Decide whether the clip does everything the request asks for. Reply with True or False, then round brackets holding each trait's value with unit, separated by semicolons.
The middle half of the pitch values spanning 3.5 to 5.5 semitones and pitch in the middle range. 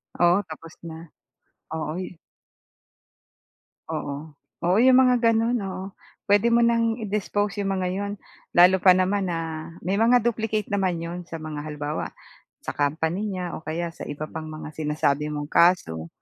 True (4.5 semitones; 180 Hz)